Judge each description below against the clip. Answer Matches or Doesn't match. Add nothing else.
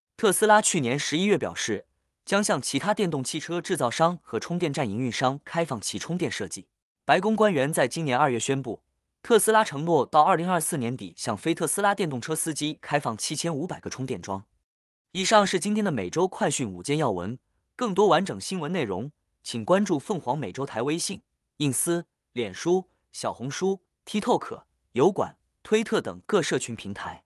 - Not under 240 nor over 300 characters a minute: Matches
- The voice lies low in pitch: Doesn't match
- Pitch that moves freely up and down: Matches